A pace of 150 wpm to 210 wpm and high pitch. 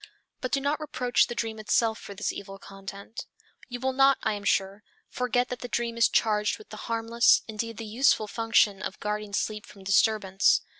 Yes: average, 195 wpm; high, 220 Hz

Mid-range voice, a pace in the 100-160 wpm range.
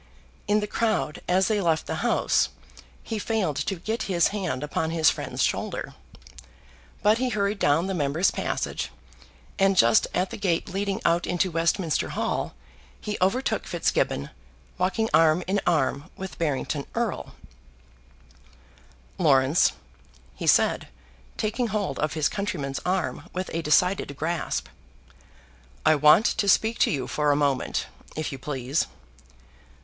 Yes: medium, 175 Hz; average, 140 wpm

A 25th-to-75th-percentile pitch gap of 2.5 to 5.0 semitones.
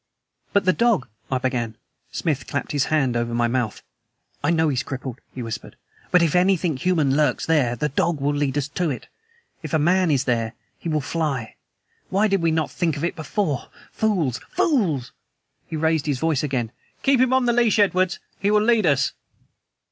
No: wide, 5.6 semitones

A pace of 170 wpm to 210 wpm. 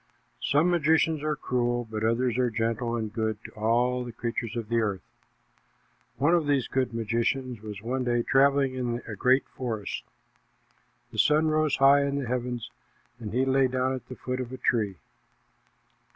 Yes: average, 175 wpm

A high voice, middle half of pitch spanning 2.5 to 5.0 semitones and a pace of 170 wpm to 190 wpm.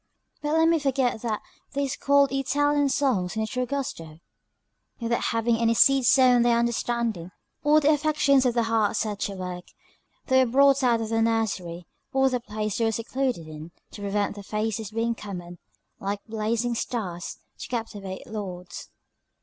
Yes: high, 230 Hz; average, 4.3 semitones; average, 175 wpm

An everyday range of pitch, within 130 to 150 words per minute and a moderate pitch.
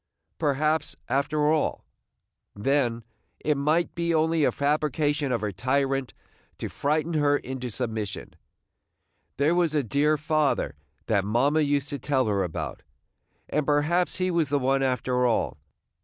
Yes: average, 3.1 semitones; average, 140 wpm; medium, 145 Hz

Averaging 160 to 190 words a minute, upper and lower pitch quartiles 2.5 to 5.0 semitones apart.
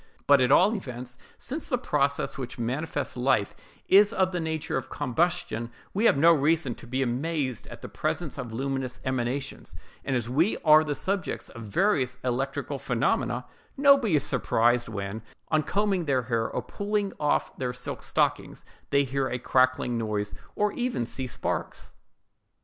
No: average, 165 wpm; wide, 5.4 semitones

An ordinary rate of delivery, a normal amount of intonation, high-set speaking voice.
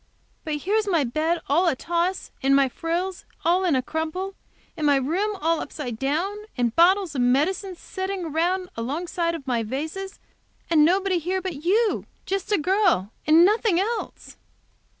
Yes: average, 170 wpm; average, 4.3 semitones; very high, 340 Hz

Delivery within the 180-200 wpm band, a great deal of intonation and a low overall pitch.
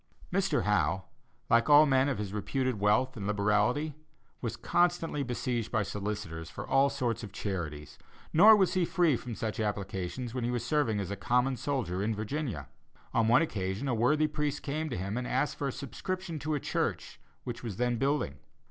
Yes: average, 190 wpm; wide, 5.8 semitones; low, 120 Hz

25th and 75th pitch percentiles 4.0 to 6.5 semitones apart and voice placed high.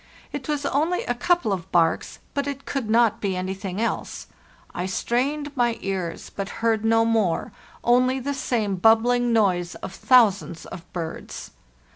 Yes: average, 5.0 semitones; high, 225 Hz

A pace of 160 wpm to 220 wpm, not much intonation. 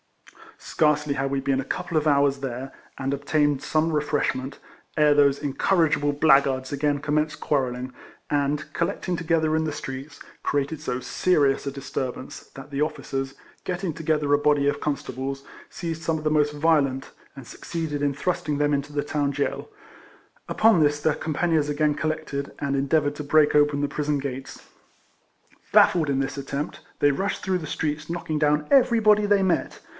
Yes: average, 170 wpm; narrow, 2.0 semitones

